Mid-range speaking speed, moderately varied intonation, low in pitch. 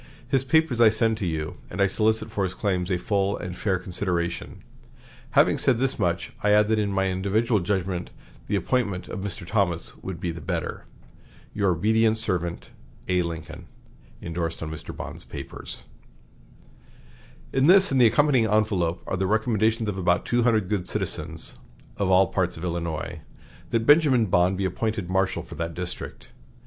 Yes: average, 170 wpm; average, 3.9 semitones; very low, 95 Hz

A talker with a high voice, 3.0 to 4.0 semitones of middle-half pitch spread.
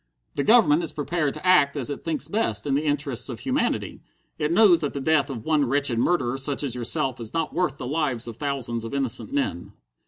No: medium, 145 Hz; average, 3.7 semitones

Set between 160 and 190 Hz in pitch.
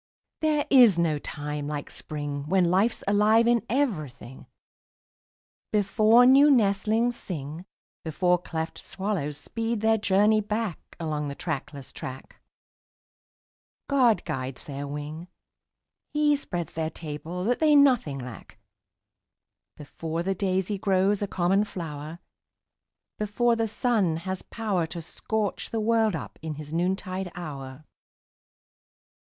Yes: medium, 185 Hz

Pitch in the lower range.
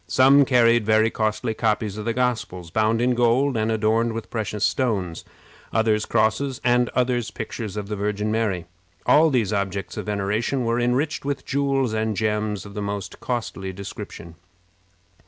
Yes: low, 110 Hz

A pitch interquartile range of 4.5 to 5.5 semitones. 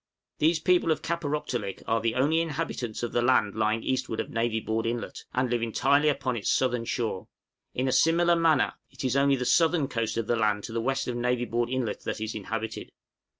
No: average, 3.9 semitones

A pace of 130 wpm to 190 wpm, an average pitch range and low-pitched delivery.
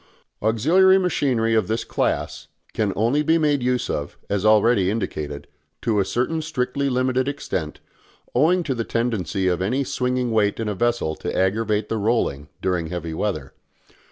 Yes: average, 160 wpm; average, 4.9 semitones; low, 115 Hz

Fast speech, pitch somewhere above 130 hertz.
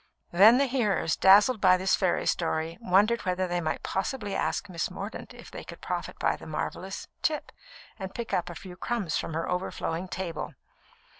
No: average, 180 wpm; high, 190 Hz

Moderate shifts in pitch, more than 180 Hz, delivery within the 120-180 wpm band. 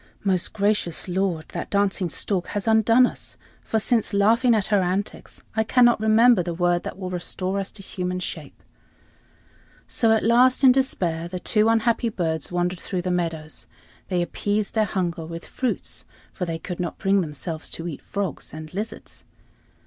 Yes: average, 3.9 semitones; high, 190 Hz; average, 170 wpm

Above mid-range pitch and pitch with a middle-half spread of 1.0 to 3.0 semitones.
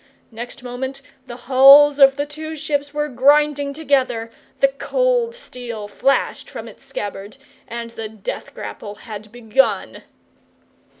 No: very high, 270 Hz; average, 3.9 semitones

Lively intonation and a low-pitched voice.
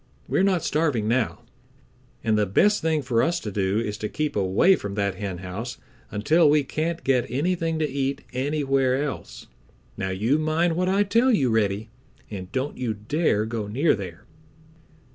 Yes: wide, 7.0 semitones; low, 130 Hz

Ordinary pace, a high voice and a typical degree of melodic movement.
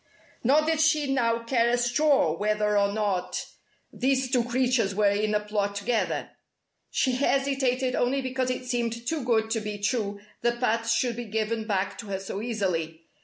Yes: average, 175 wpm; high, 230 Hz; average, 3.4 semitones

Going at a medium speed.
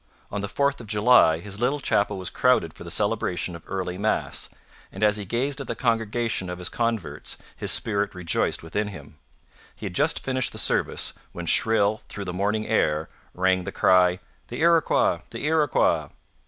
Yes: average, 180 wpm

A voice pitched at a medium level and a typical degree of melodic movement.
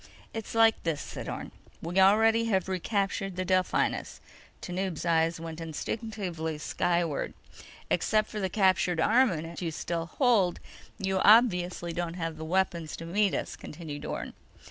Yes: medium, 180 Hz; average, 3.5 semitones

